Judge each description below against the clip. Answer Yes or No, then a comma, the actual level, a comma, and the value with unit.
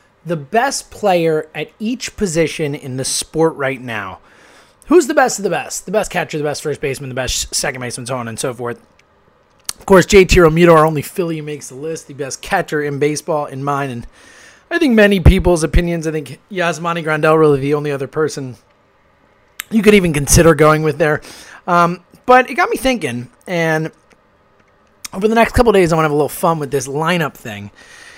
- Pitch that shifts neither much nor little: Yes, average, 4.3 semitones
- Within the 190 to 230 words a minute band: Yes, fast, 205 wpm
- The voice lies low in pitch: No, medium, 155 Hz